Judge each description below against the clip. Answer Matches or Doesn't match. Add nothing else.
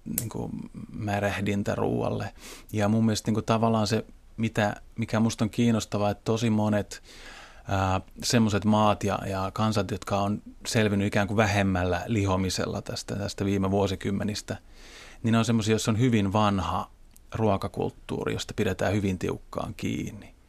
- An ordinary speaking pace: Matches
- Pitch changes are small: Matches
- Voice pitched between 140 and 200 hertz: Doesn't match